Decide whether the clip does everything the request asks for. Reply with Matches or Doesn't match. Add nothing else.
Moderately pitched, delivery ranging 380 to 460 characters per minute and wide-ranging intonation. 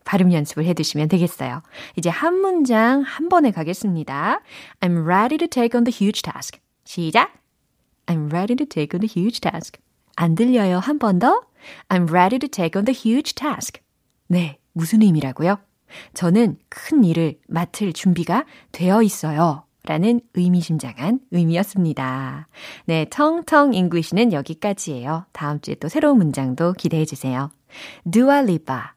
Matches